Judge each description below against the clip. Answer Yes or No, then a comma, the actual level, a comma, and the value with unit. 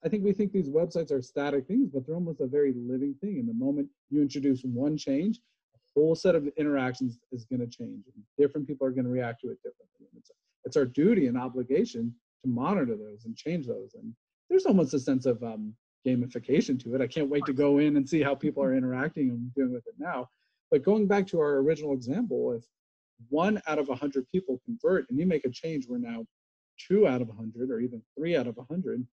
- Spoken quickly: Yes, fast, 230 wpm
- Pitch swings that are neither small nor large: No, wide, 6.6 semitones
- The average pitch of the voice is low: No, medium, 145 Hz